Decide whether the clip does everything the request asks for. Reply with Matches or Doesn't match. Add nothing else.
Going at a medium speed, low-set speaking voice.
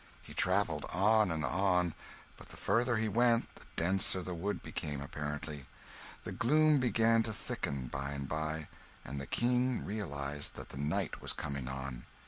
Matches